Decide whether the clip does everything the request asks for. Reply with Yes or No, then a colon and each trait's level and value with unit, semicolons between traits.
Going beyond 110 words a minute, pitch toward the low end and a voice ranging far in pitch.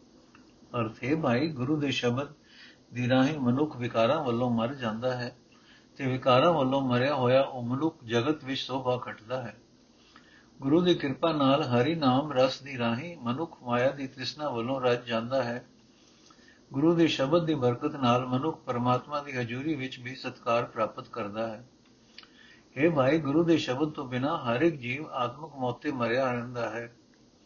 No: average, 160 wpm; low, 130 Hz; average, 3.4 semitones